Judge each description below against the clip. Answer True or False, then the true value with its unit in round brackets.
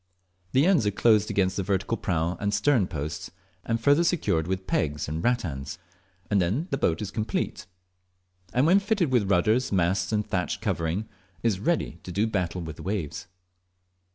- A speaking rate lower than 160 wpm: False (175 wpm)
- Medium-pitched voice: False (100 Hz)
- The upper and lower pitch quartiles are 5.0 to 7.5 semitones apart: True (5.5 semitones)